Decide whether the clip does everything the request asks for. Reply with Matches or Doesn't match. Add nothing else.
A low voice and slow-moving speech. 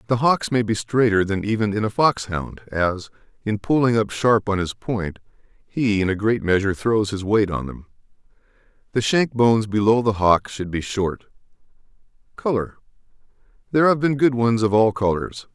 Doesn't match